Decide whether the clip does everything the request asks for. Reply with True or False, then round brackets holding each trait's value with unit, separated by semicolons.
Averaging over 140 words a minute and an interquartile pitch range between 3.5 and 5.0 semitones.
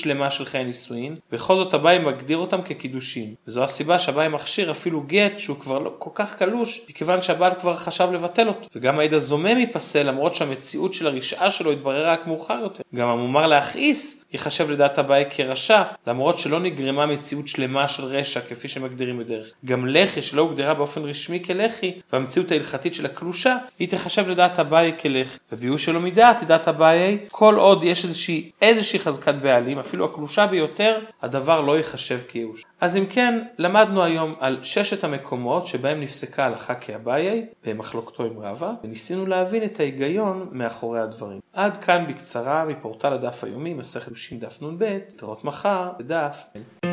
False (150 wpm; 5.4 semitones)